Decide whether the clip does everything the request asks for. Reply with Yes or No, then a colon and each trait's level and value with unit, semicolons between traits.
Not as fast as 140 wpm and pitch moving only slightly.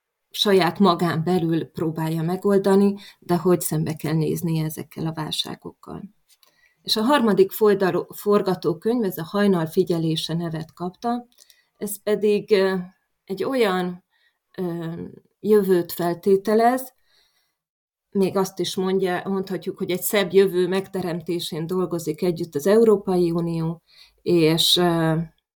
No: slow, 105 wpm; average, 3.0 semitones